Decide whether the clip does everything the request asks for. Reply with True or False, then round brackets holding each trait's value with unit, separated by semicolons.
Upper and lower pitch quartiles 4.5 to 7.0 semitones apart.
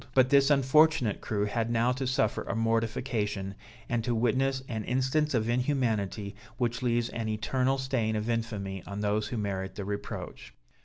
False (3.5 semitones)